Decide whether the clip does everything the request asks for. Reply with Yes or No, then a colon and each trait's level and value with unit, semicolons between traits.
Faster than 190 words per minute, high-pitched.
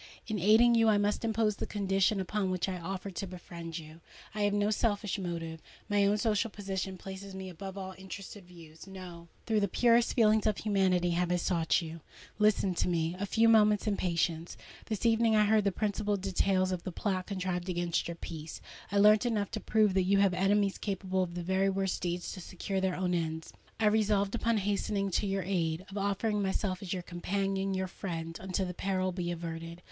Yes: average, 200 wpm; high, 195 Hz